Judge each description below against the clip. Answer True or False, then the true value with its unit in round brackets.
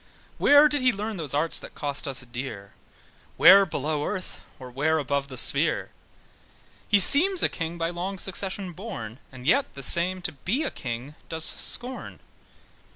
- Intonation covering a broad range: True (6.4 semitones)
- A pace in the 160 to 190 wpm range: True (165 wpm)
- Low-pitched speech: False (165 Hz)